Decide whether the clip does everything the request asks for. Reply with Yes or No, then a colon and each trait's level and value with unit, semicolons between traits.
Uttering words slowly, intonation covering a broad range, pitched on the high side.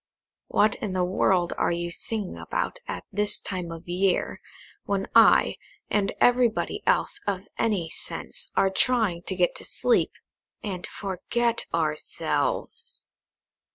No: slow, 130 wpm; average, 3.5 semitones; high, 195 Hz